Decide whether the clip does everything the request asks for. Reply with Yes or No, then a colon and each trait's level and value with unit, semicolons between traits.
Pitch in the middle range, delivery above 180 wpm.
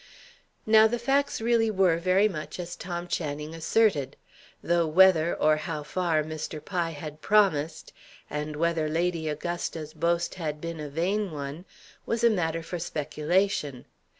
No: medium, 170 Hz; average, 150 wpm